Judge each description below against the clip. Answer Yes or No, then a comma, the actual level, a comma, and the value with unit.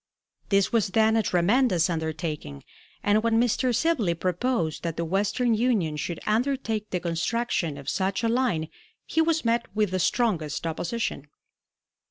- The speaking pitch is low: No, high, 205 Hz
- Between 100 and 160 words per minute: Yes, average, 150 wpm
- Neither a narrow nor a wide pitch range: No, wide, 5.8 semitones